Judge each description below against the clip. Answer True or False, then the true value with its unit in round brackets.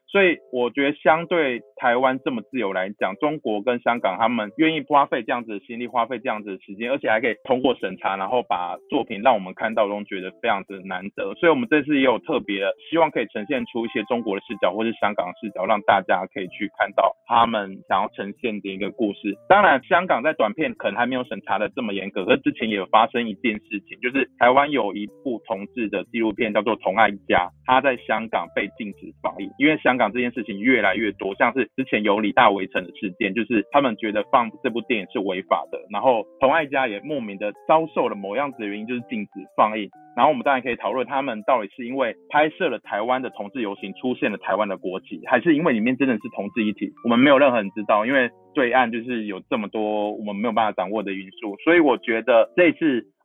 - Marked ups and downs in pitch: False (4.6 semitones)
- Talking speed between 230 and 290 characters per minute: False (365 characters per minute)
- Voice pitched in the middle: False (115 Hz)